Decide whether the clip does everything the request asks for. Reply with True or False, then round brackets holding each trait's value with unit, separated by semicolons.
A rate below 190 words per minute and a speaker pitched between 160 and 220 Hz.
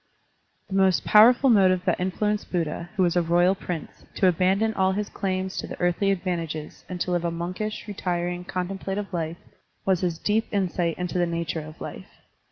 True (180 wpm; 185 Hz)